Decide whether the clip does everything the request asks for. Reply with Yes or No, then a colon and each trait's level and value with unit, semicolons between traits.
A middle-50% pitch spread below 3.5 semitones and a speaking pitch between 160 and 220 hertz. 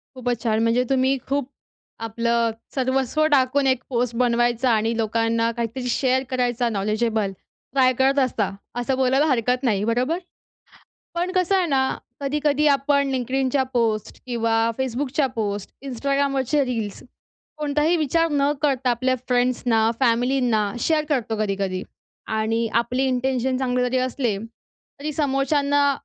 No: average, 3.0 semitones; very high, 255 Hz